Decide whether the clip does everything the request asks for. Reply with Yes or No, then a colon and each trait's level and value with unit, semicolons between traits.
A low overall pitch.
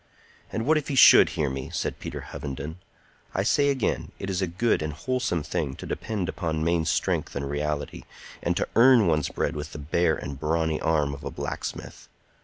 Yes: very low, 80 Hz